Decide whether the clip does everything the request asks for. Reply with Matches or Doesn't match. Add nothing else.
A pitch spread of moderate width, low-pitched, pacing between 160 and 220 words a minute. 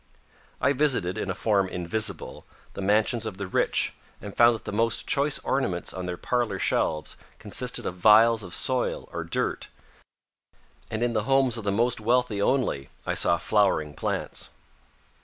Matches